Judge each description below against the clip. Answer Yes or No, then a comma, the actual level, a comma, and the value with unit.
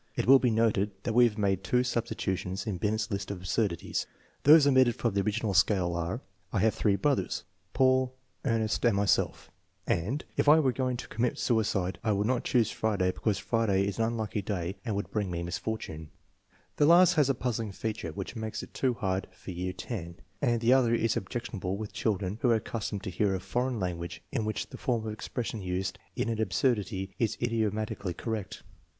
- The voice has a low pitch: Yes, low, 110 Hz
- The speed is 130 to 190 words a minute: No, fast, 205 wpm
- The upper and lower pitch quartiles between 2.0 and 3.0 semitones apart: No, average, 3.7 semitones